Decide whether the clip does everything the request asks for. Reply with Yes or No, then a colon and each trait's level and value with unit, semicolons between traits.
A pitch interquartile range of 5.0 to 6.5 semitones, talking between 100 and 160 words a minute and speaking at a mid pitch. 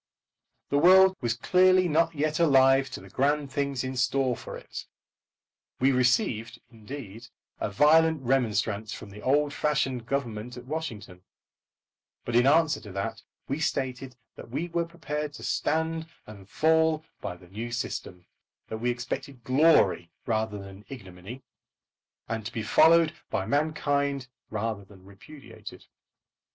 No: average, 5.3 semitones; average, 140 wpm; low, 130 Hz